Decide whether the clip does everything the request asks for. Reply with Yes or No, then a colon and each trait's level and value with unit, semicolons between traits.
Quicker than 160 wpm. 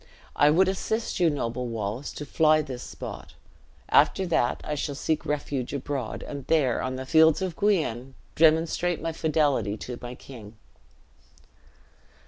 No: average, 145 wpm